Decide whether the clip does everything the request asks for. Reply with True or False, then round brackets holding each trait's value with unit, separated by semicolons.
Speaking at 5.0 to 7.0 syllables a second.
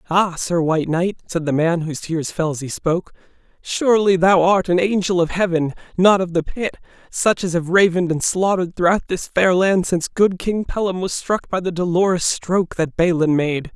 True (5.3 syllables/s)